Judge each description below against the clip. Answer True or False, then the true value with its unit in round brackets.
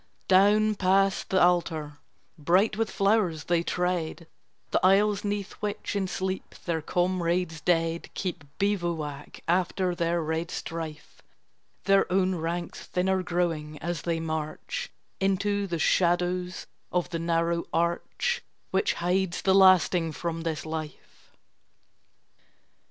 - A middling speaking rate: False (120 wpm)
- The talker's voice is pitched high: False (175 Hz)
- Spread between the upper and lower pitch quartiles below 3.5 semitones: True (2.5 semitones)